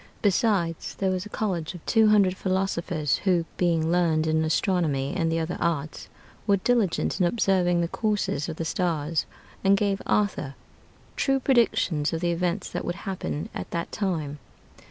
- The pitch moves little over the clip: No, average, 3.3 semitones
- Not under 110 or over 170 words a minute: Yes, average, 165 wpm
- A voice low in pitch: No, medium, 175 Hz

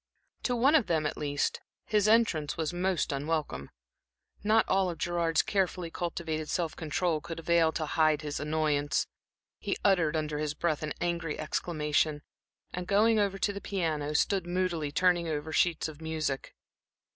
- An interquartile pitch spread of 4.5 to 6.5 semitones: No, average, 3.1 semitones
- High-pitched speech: No, medium, 165 Hz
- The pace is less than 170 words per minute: Yes, average, 160 wpm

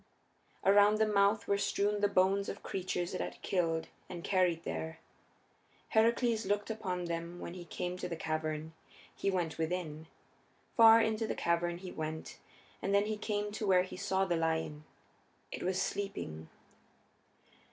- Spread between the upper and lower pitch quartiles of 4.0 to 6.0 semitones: No, average, 3.5 semitones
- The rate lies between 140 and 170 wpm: Yes, average, 160 wpm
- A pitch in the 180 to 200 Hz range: Yes, medium, 185 Hz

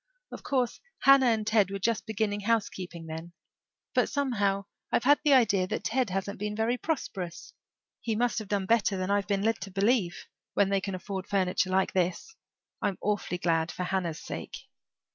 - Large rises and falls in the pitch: No, average, 3.4 semitones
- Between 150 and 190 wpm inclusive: Yes, average, 180 wpm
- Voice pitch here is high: Yes, high, 200 Hz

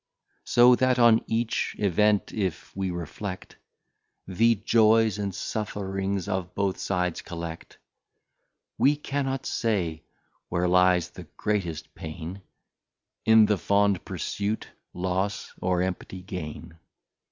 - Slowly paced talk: Yes, slow, 110 wpm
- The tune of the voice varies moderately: Yes, average, 3.2 semitones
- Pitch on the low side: Yes, very low, 95 Hz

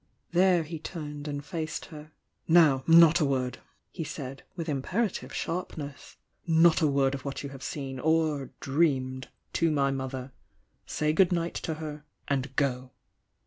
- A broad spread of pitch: No, average, 3.2 semitones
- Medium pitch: Yes, medium, 150 Hz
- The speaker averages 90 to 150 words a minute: No, average, 165 wpm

